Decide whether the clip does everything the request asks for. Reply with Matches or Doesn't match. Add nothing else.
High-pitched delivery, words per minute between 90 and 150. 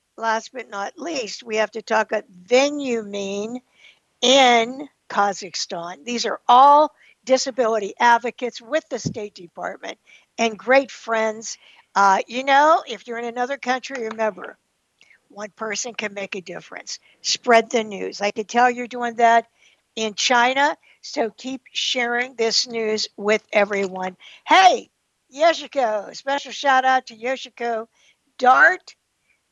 Matches